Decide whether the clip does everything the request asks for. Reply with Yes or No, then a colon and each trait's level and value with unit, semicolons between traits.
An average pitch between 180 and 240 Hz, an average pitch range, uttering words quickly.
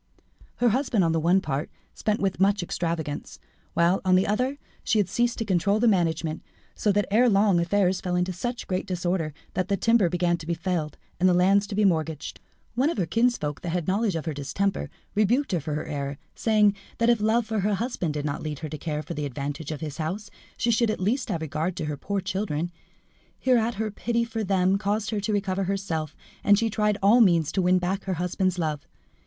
Yes: high, 190 Hz; average, 4.4 semitones; fast, 225 wpm